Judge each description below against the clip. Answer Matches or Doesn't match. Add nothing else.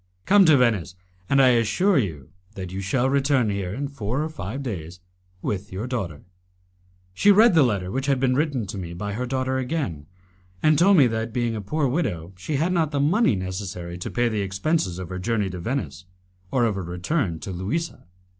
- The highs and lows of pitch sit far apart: Matches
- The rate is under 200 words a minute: Doesn't match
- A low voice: Matches